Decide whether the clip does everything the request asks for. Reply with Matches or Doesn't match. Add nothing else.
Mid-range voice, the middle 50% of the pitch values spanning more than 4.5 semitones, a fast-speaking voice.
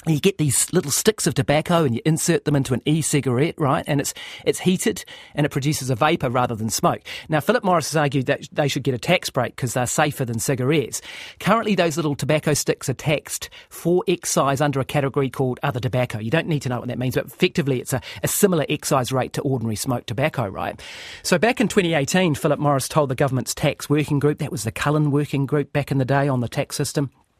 Doesn't match